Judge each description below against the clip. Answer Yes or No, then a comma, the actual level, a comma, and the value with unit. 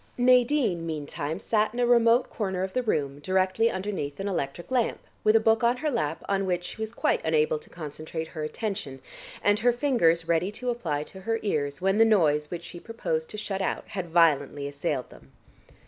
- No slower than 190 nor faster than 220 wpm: Yes, average, 200 wpm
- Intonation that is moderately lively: No, wide, 6.2 semitones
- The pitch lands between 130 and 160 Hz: No, high, 190 Hz